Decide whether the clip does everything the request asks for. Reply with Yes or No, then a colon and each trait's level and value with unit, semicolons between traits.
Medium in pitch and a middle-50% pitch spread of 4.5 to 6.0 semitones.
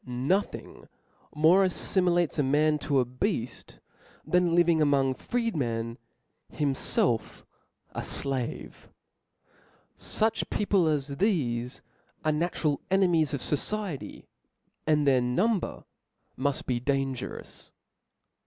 Yes: medium, 150 Hz; average, 5.2 semitones